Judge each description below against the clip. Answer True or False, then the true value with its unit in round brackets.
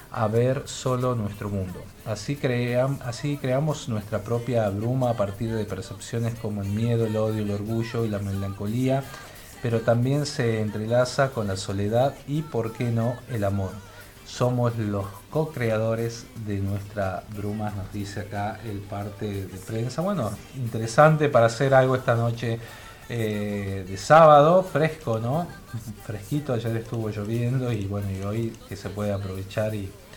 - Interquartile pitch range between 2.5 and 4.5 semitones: True (3.3 semitones)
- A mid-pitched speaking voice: False (115 Hz)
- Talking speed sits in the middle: True (155 wpm)